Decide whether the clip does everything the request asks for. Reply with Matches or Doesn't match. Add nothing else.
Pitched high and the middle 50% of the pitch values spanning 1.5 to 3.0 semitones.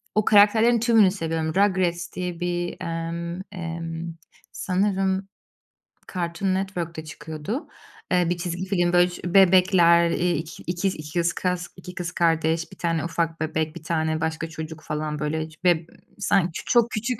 Doesn't match